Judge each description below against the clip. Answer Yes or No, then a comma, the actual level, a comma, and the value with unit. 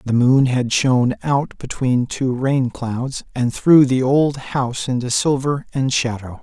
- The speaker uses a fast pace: No, average, 170 wpm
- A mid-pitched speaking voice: No, low, 130 Hz